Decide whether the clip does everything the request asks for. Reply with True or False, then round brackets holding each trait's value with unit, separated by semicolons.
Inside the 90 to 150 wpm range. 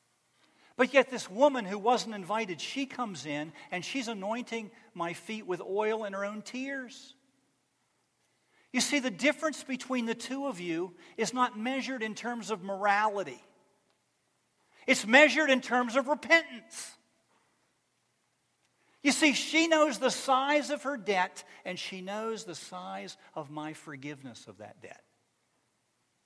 True (145 wpm)